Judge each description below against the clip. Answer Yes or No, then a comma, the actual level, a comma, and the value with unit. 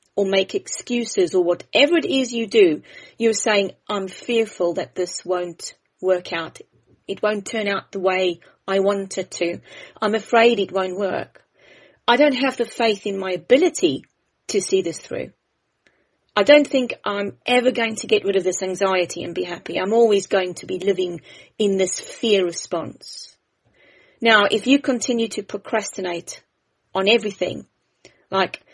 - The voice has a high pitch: Yes, high, 205 Hz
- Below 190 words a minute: Yes, average, 165 wpm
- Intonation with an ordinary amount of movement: Yes, average, 3.7 semitones